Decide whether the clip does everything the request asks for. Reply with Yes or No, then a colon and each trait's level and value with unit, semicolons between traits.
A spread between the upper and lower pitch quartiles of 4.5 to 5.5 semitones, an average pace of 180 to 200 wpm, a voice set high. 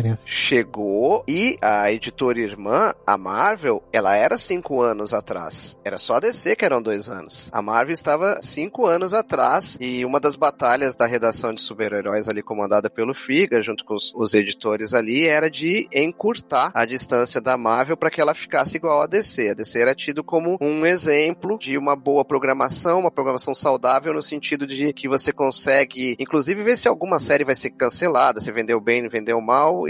No: average, 4.8 semitones; fast, 185 wpm; low, 135 Hz